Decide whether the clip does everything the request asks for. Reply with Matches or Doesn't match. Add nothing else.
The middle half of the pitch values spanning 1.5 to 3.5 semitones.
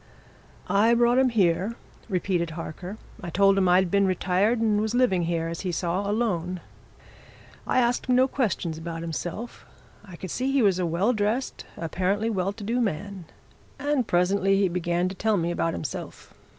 Doesn't match